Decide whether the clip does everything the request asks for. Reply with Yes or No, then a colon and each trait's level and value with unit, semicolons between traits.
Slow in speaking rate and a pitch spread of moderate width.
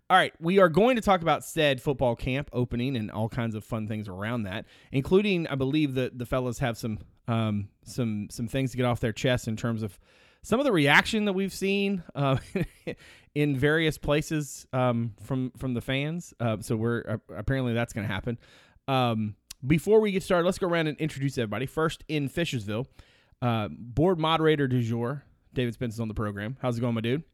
No: fast, 205 wpm; average, 4.6 semitones